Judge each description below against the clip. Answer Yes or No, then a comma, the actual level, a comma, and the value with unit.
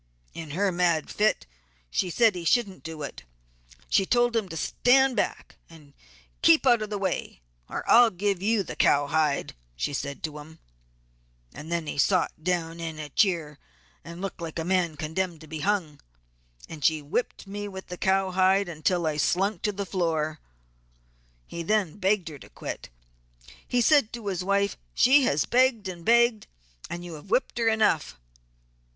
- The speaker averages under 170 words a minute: No, average, 175 wpm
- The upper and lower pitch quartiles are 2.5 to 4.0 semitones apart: No, average, 4.5 semitones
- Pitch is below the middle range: No, medium, 180 Hz